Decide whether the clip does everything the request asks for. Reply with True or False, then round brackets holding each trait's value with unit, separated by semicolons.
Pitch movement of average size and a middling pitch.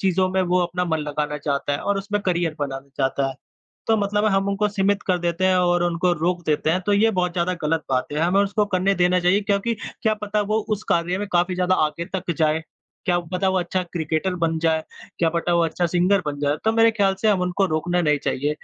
True (3.4 semitones; 180 Hz)